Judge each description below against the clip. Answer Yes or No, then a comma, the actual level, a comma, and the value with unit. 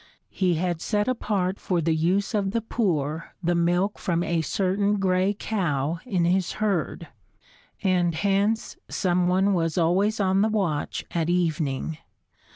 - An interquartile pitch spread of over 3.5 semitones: No, average, 3.0 semitones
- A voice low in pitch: No, medium, 180 Hz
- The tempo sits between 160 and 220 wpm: No, average, 150 wpm